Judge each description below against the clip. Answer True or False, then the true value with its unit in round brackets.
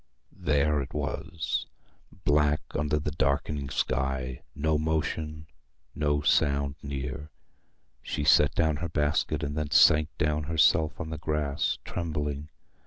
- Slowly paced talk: True (125 wpm)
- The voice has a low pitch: True (75 Hz)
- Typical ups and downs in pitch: False (1.4 semitones)